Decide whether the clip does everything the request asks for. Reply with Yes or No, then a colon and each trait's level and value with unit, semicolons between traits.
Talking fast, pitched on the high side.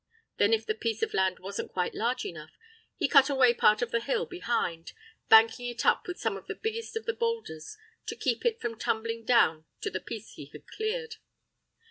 Yes: fast, 210 wpm; high, 235 Hz